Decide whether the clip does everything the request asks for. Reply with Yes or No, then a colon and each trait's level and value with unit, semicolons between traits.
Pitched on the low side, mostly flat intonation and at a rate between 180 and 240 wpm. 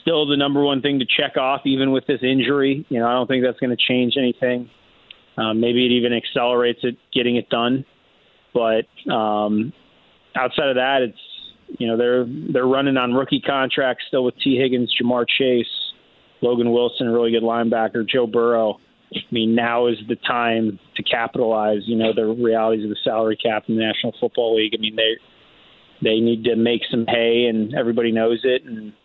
Yes: low, 120 Hz; narrow, 2.1 semitones; average, 195 wpm